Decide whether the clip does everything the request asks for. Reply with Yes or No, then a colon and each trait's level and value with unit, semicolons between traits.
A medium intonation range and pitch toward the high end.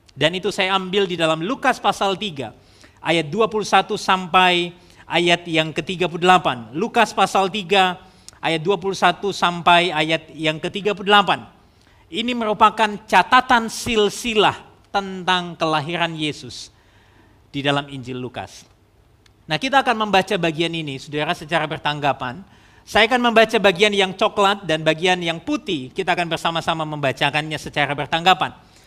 No: average, 5.0 semitones; medium, 175 Hz